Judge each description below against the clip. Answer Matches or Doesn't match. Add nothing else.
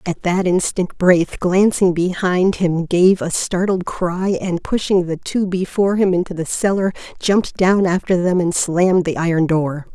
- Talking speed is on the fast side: Doesn't match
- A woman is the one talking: Matches